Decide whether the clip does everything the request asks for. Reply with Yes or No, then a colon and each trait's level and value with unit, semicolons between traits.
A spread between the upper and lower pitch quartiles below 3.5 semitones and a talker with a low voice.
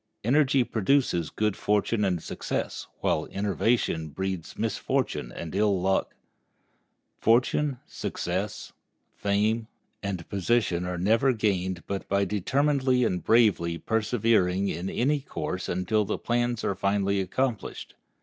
No: average, 4.2 semitones; low, 105 Hz